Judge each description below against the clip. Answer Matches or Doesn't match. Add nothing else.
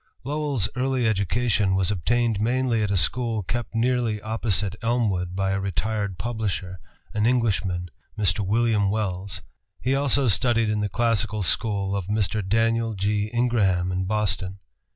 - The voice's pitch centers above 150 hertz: Doesn't match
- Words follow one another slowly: Doesn't match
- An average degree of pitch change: Matches